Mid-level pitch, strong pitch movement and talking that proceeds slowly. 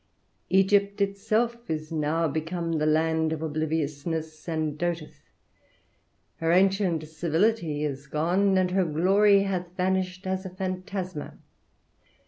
No: medium, 175 Hz; average, 3.3 semitones; slow, 115 wpm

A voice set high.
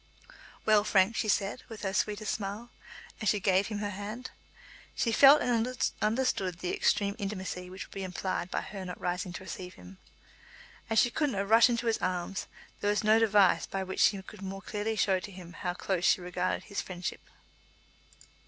Yes: high, 200 Hz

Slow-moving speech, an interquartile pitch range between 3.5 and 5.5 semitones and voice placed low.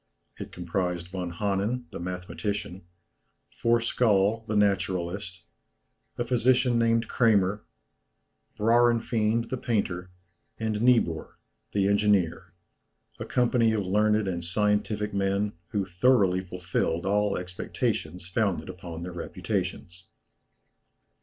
Yes: slow, 100 wpm; average, 3.8 semitones; low, 100 Hz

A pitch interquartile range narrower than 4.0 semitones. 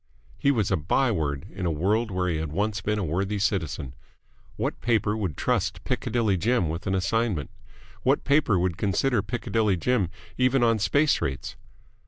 No: average, 4.8 semitones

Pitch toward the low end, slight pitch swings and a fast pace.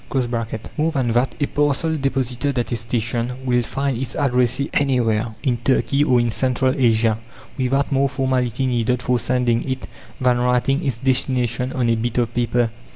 No: low, 125 Hz; narrow, 2.1 semitones; average, 165 wpm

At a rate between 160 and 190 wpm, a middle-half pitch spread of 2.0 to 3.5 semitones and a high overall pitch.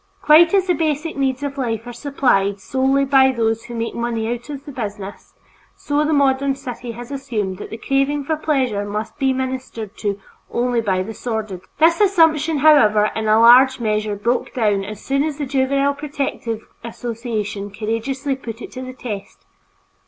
No: average, 180 wpm; average, 4.1 semitones; very high, 250 Hz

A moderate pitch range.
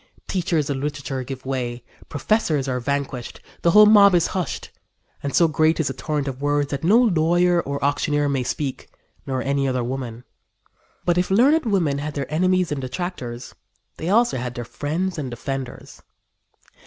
Yes: average, 4.8 semitones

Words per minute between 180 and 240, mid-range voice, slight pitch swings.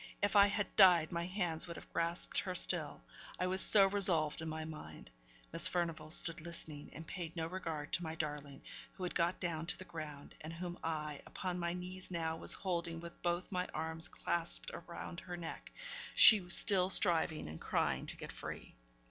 Yes: average, 190 wpm; medium, 170 Hz; narrow, 2.2 semitones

